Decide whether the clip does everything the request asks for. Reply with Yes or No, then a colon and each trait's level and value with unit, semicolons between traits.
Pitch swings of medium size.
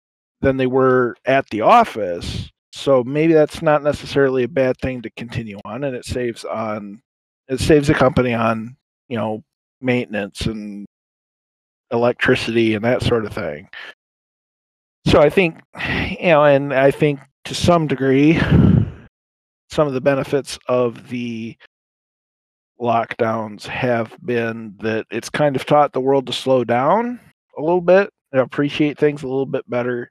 Yes: average, 3.7 semitones